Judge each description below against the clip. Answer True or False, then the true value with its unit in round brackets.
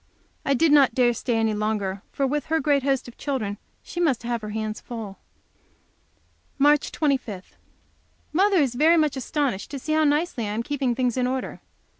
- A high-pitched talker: True (260 Hz)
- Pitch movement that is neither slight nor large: True (4.6 semitones)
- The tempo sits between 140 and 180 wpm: False (190 wpm)